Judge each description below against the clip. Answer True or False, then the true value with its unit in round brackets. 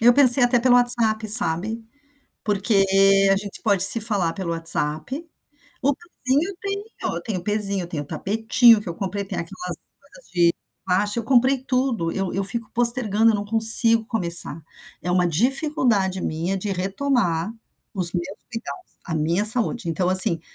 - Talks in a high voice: True (210 Hz)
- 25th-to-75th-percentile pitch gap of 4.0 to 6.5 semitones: True (4.7 semitones)